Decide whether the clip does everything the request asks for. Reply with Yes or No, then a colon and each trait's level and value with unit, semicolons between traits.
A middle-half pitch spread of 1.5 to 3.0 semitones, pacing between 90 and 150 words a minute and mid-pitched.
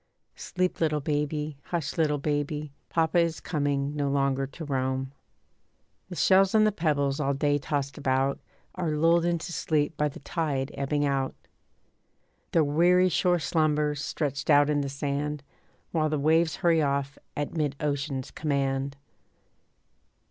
Yes: narrow, 2.5 semitones; average, 145 wpm; medium, 150 Hz